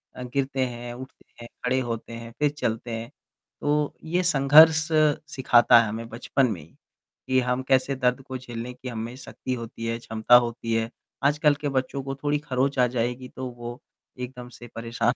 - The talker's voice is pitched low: Yes, low, 125 Hz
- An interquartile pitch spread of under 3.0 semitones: Yes, narrow, 2.5 semitones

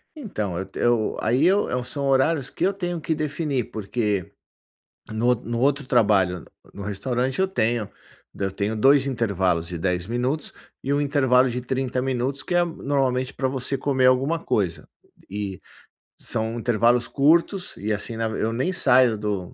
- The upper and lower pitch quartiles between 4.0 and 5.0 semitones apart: Yes, average, 4.5 semitones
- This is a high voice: No, low, 125 Hz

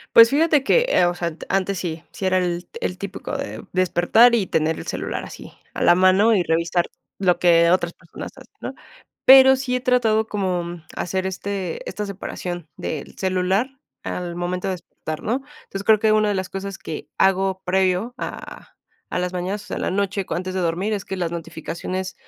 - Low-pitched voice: No, medium, 185 Hz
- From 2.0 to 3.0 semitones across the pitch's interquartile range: Yes, average, 2.7 semitones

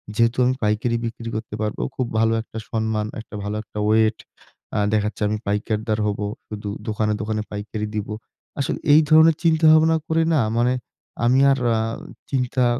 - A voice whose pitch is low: Yes, low, 110 Hz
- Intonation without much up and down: No, average, 3.2 semitones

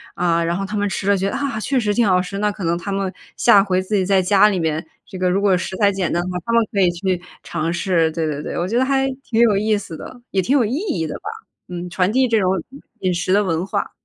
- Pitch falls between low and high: No, high, 195 Hz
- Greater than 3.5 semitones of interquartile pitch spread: No, average, 3.0 semitones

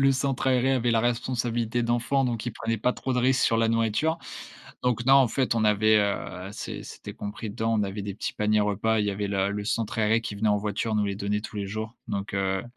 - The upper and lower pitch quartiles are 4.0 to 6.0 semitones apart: No, average, 2.7 semitones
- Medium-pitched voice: No, low, 110 Hz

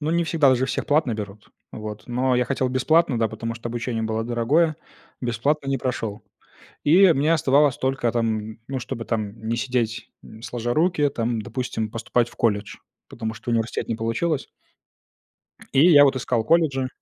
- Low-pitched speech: Yes, low, 120 Hz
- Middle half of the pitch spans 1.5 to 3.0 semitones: No, average, 3.7 semitones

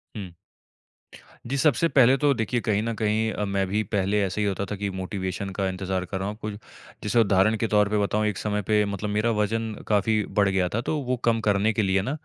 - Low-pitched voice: Yes, low, 105 Hz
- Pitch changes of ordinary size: No, narrow, 2.3 semitones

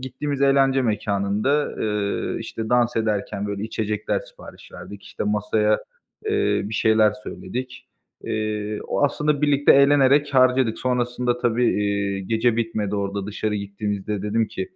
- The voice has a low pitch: Yes, low, 110 Hz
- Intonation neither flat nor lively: Yes, average, 3.8 semitones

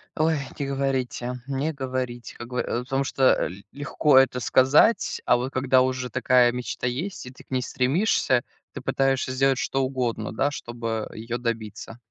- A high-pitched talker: No, low, 130 Hz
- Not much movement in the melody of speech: Yes, narrow, 1.8 semitones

